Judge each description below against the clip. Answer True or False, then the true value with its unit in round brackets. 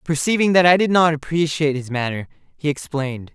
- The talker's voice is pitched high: False (150 Hz)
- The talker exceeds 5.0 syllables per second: True (6.0 syllables/s)